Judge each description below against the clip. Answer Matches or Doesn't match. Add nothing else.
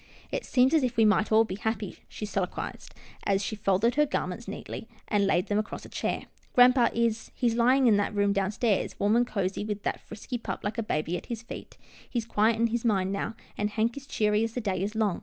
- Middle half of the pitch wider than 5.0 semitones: Doesn't match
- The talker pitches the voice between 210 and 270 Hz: Matches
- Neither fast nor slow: Doesn't match